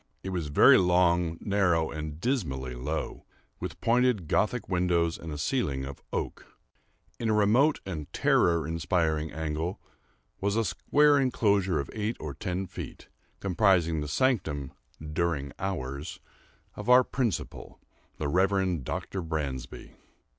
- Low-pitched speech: Yes, very low, 85 Hz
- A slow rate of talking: Yes, slow, 130 wpm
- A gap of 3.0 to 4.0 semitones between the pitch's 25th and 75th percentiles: No, average, 4.9 semitones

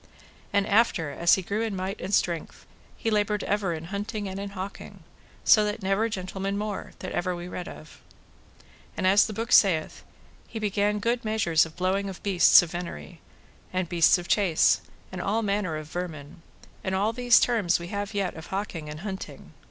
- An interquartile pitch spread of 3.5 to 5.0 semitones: No, average, 3.0 semitones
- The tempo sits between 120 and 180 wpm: No, average, 190 wpm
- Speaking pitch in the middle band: No, high, 195 Hz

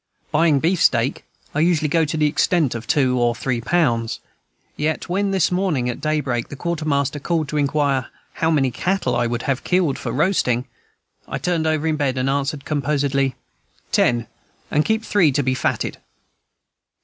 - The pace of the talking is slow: No, average, 170 wpm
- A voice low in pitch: No, medium, 145 Hz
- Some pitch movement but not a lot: Yes, average, 3.8 semitones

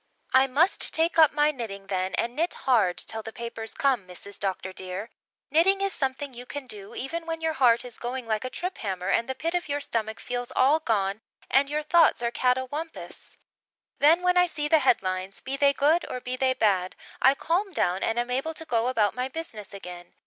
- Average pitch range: No, wide, 5.7 semitones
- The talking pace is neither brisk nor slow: No, fast, 215 wpm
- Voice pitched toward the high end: Yes, very high, 255 Hz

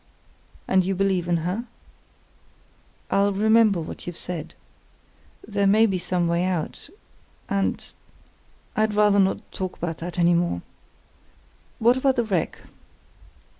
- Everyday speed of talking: No, slow, 125 wpm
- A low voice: No, high, 190 Hz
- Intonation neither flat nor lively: Yes, average, 3.1 semitones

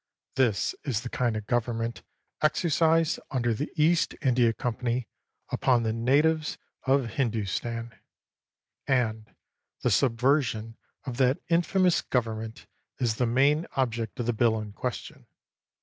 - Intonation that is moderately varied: Yes, average, 3.4 semitones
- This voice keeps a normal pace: No, slow, 125 wpm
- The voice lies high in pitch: No, low, 120 Hz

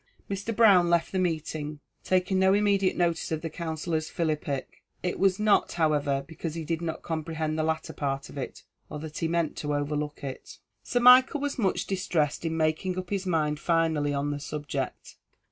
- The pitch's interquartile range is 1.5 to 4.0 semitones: Yes, average, 3.6 semitones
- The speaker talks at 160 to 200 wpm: Yes, average, 185 wpm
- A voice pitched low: No, medium, 160 Hz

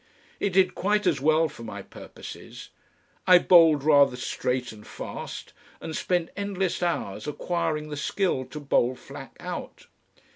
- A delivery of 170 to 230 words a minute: No, average, 145 wpm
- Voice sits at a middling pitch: Yes, medium, 155 Hz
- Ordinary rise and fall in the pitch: Yes, average, 4.7 semitones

